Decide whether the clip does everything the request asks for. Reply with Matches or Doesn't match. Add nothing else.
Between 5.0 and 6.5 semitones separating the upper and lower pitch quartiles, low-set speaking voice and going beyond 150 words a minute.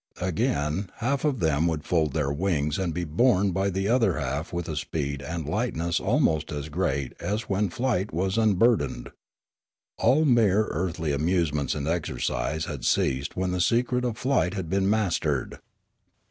Matches